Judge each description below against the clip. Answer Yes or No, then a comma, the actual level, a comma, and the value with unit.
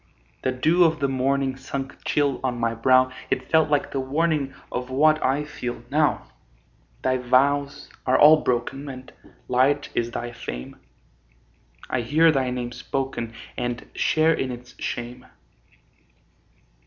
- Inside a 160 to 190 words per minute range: No, average, 140 wpm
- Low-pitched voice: Yes, low, 130 Hz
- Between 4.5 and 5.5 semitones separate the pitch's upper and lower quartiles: No, narrow, 2.4 semitones